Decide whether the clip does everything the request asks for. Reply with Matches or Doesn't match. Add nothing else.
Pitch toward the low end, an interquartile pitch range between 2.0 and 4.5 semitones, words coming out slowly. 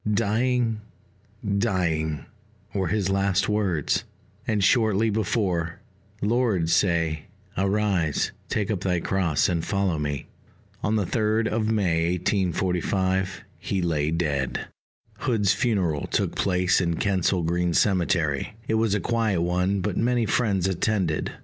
Matches